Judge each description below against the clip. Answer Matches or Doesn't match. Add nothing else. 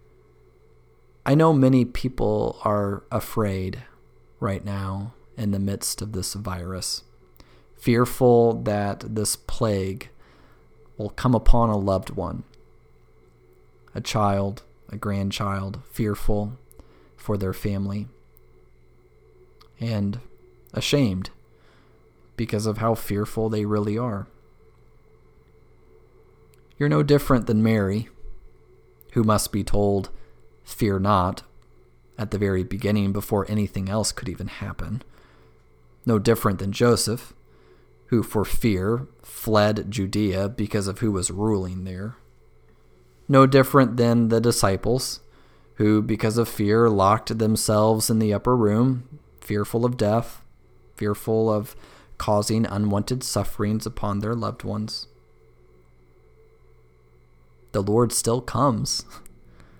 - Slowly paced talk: Matches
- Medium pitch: Doesn't match